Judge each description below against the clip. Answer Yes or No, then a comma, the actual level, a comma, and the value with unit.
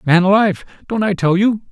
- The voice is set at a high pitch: Yes, high, 195 Hz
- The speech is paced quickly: Yes, fast, 210 wpm